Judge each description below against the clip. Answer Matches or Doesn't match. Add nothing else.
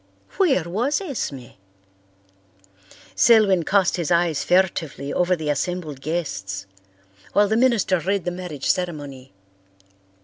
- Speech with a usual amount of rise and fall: Matches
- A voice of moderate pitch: Matches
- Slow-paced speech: Matches